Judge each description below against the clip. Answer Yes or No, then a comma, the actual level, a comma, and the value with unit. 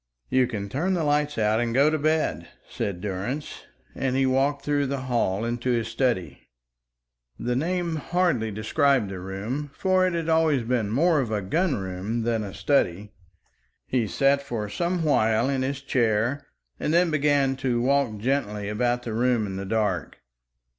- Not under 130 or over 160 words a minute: No, average, 175 wpm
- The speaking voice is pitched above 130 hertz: No, low, 125 Hz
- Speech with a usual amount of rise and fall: Yes, average, 5.0 semitones